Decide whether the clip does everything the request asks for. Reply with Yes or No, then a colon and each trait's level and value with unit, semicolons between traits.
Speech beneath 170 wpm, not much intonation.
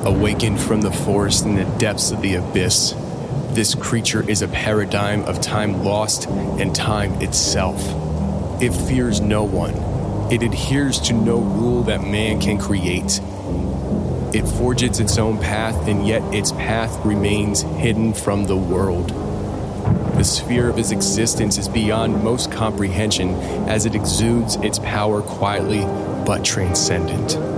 Yes: average, 140 wpm; narrow, 2.2 semitones